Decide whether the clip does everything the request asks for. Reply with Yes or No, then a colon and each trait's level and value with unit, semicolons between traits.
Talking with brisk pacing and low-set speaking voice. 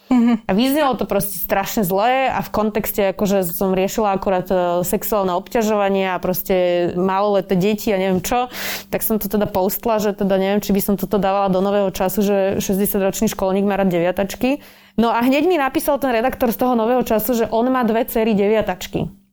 No: fast, 190 wpm; high, 205 Hz